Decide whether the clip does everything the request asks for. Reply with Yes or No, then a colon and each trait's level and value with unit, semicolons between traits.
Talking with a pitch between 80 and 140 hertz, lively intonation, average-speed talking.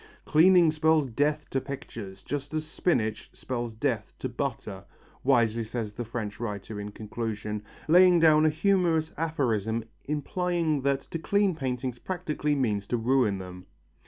Yes: low, 135 Hz; wide, 6.1 semitones; average, 145 wpm